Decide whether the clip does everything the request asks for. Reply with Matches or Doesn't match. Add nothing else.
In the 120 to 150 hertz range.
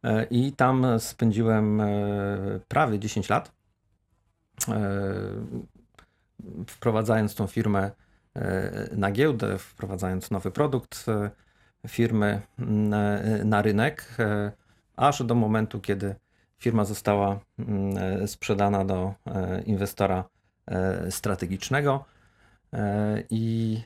Doesn't match